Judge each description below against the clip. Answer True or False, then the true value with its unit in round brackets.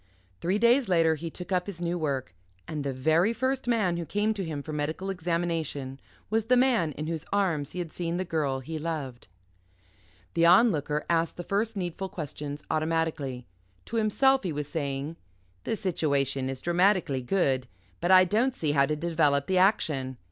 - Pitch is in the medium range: True (165 Hz)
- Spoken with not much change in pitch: False (4.7 semitones)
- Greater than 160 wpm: True (180 wpm)